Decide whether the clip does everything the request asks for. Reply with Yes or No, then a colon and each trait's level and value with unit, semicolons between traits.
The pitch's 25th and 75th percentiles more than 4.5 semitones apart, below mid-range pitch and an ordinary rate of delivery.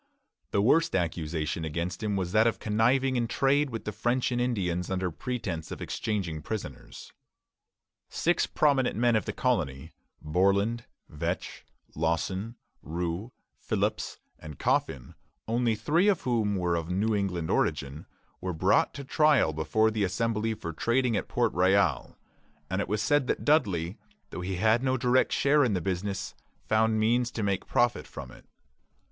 Yes: average, 5.3 semitones; low, 105 Hz; average, 160 wpm